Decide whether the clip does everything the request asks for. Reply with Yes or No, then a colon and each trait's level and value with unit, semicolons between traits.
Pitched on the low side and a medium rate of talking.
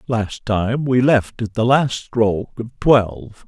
Yes: low, 115 Hz; average, 175 wpm